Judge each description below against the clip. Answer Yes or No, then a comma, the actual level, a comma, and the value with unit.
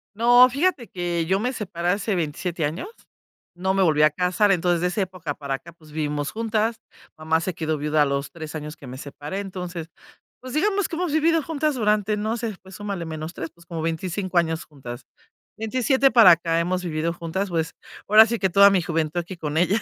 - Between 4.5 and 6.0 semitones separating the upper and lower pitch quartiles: Yes, average, 5.0 semitones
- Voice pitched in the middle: Yes, medium, 180 Hz